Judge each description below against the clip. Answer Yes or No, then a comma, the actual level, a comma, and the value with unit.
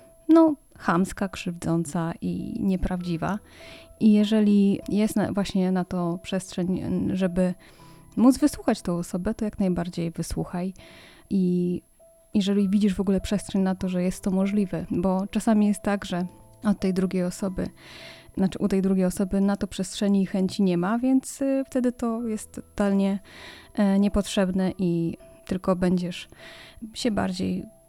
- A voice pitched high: Yes, high, 195 Hz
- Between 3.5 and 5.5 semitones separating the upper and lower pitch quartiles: No, narrow, 2.6 semitones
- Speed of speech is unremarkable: Yes, average, 140 wpm